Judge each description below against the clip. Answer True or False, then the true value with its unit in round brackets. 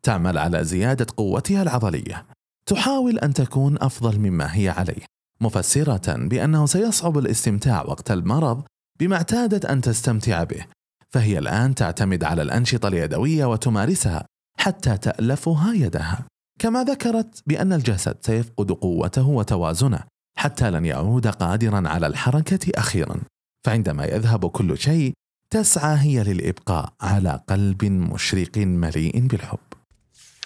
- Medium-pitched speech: False (120 Hz)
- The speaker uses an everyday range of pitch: False (6.9 semitones)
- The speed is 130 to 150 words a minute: False (115 wpm)